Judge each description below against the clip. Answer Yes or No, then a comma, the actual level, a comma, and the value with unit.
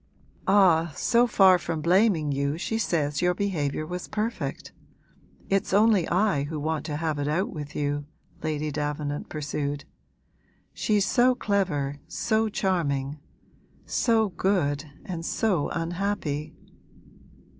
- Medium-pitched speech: Yes, medium, 165 Hz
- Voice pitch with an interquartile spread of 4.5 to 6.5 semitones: Yes, average, 5.2 semitones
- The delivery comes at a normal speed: No, slow, 125 wpm